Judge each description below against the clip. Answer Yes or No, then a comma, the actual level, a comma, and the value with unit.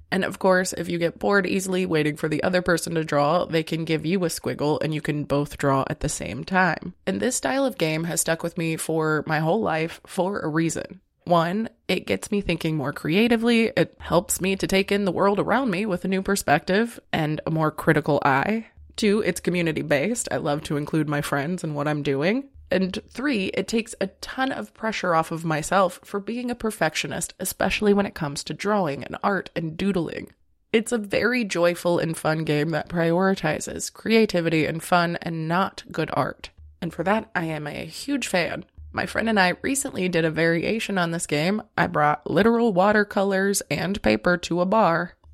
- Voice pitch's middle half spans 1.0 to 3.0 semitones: No, average, 4.2 semitones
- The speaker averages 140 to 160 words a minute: No, fast, 205 wpm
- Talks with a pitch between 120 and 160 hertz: No, medium, 175 Hz